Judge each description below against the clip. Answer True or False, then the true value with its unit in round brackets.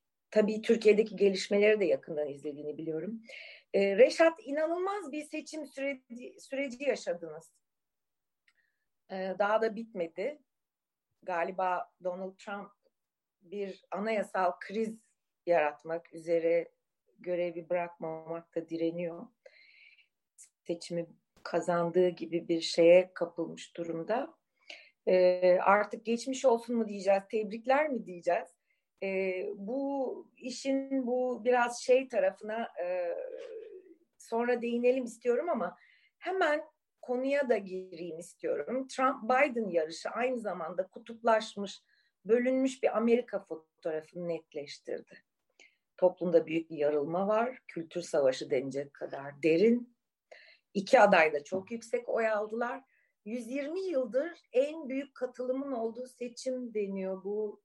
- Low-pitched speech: False (220 Hz)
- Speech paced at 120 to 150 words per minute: False (105 wpm)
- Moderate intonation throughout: False (6.8 semitones)